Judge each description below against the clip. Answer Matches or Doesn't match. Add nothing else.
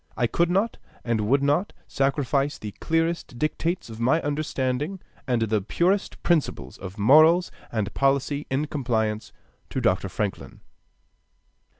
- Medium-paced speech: Doesn't match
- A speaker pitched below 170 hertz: Matches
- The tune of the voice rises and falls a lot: Matches